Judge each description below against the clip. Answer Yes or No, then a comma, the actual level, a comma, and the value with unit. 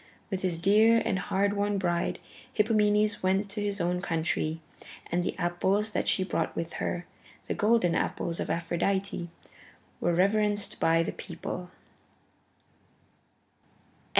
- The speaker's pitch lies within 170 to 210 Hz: Yes, high, 190 Hz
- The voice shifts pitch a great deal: No, average, 3.1 semitones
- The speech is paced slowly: Yes, slow, 130 wpm